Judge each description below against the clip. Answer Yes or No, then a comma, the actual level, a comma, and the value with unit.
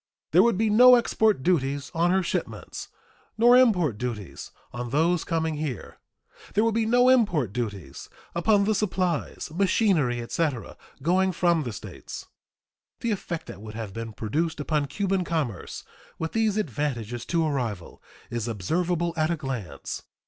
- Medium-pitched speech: Yes, medium, 160 Hz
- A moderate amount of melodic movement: No, wide, 7.9 semitones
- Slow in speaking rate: No, average, 155 wpm